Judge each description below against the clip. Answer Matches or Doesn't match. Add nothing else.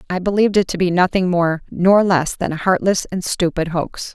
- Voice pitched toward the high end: Doesn't match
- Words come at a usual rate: Doesn't match